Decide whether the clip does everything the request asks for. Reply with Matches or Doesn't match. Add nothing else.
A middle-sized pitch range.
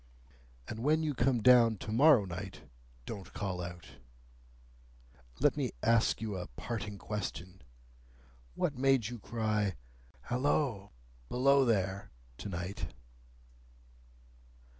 Matches